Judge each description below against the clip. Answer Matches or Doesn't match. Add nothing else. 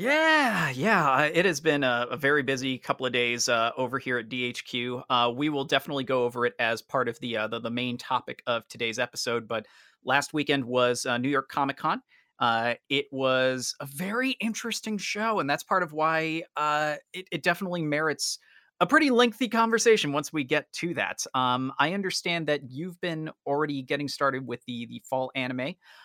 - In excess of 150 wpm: Matches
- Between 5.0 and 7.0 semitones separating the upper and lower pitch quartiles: Matches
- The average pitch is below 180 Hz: Matches